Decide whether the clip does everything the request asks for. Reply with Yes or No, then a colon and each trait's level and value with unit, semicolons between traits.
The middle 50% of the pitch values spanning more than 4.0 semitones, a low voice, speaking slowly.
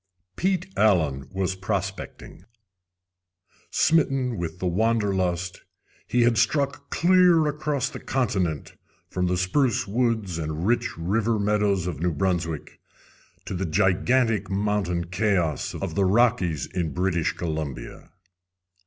Yes: average, 5.1 semitones; very low, 95 Hz; slow, 120 wpm